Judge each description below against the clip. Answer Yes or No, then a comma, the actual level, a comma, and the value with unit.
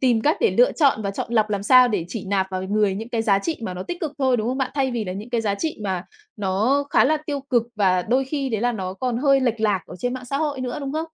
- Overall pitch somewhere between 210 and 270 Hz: Yes, high, 235 Hz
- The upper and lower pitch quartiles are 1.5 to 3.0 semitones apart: No, average, 5.0 semitones